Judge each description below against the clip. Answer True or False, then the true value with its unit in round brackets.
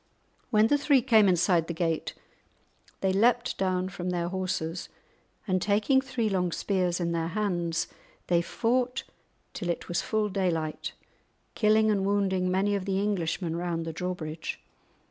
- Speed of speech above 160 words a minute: False (150 wpm)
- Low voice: False (185 Hz)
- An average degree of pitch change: True (3.5 semitones)